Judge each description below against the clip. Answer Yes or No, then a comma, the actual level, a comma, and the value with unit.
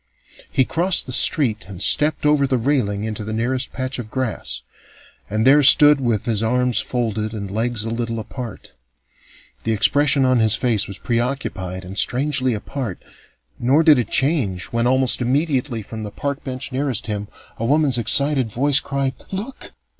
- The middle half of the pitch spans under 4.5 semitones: Yes, average, 4.0 semitones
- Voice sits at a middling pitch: No, low, 125 Hz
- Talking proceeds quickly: No, average, 165 wpm